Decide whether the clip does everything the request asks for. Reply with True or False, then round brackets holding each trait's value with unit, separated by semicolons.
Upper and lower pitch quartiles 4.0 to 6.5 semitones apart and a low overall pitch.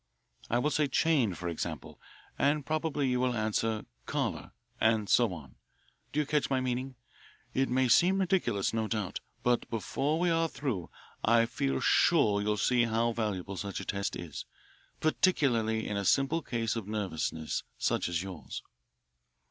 True (5.2 semitones; 115 Hz)